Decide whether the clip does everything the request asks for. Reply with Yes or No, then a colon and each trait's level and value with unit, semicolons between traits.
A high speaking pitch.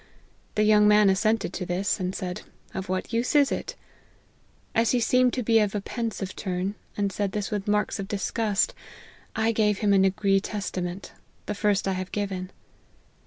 Yes: high, 205 Hz